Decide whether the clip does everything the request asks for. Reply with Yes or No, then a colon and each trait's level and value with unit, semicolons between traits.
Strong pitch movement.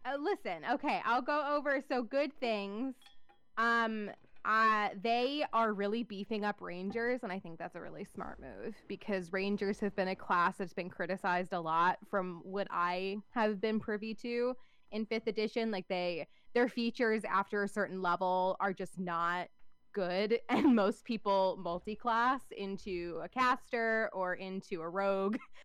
No: average, 3.6 semitones